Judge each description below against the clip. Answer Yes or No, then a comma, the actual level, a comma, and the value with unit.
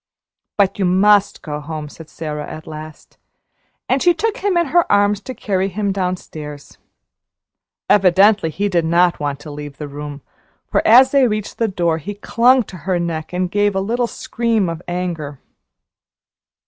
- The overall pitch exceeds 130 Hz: Yes, medium, 185 Hz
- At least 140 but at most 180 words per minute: Yes, average, 170 wpm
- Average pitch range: Yes, average, 4.9 semitones